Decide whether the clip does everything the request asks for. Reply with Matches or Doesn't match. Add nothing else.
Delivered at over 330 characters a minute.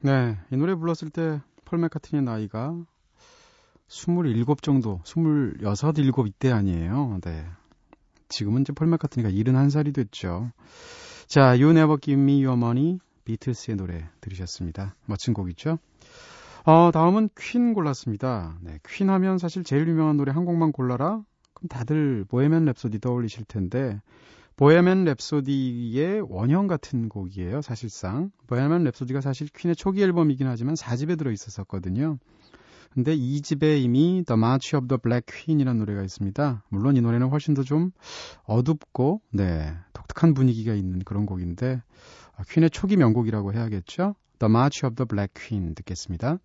Matches